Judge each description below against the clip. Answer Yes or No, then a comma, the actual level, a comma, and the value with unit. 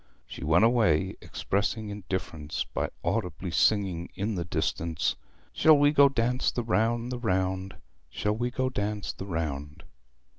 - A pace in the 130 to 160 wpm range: Yes, average, 155 wpm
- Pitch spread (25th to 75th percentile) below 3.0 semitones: No, wide, 5.5 semitones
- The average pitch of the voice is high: No, low, 100 Hz